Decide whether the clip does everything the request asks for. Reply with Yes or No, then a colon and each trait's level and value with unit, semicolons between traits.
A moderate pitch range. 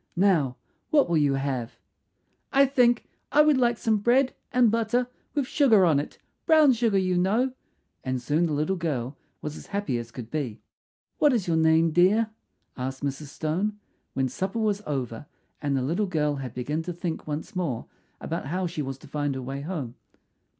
No: wide, 7.7 semitones